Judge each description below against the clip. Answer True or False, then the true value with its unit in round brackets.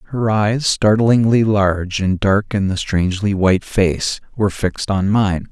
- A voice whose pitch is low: True (100 Hz)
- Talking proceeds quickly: False (165 wpm)